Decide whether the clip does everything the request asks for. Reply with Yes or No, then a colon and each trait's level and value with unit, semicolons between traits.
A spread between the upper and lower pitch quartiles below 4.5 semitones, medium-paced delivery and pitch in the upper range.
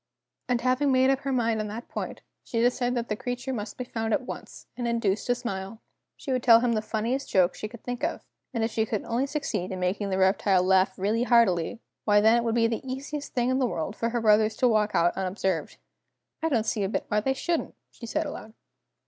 No: average, 3.2 semitones; fast, 240 wpm; high, 230 Hz